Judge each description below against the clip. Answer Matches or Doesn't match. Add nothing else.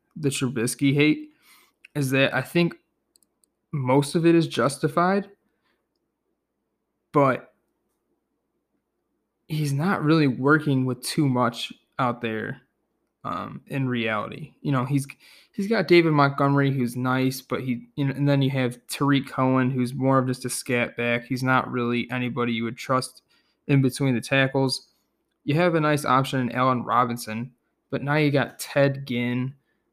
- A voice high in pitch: Doesn't match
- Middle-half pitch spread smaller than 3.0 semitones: Matches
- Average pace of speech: Matches